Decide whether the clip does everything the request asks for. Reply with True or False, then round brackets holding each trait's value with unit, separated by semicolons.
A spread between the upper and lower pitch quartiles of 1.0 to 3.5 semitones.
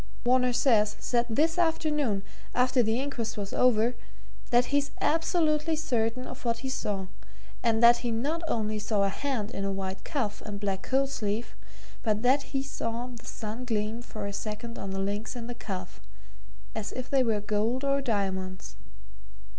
False (3.9 semitones)